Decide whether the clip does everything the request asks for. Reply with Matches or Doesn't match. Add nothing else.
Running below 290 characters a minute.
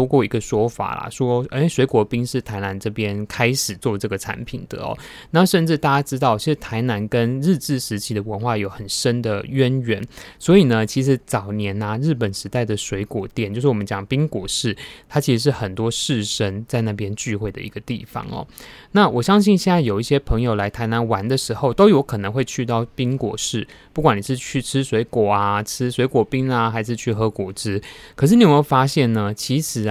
Doesn't match